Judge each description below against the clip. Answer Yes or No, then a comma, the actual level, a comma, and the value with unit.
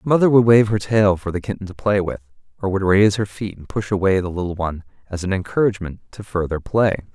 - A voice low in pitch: Yes, low, 100 Hz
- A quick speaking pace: Yes, fast, 245 wpm